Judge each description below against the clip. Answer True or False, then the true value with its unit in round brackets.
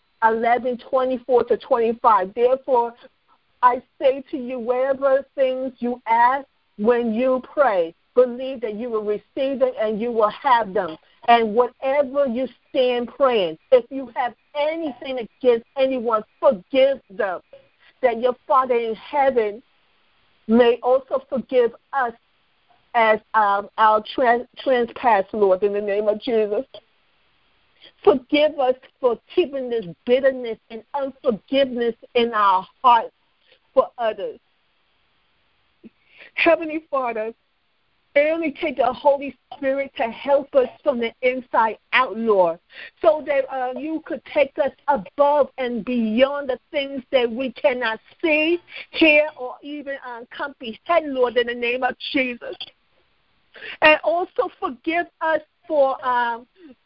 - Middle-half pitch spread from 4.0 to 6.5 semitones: False (3.4 semitones)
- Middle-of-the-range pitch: False (255 Hz)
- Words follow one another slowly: True (125 wpm)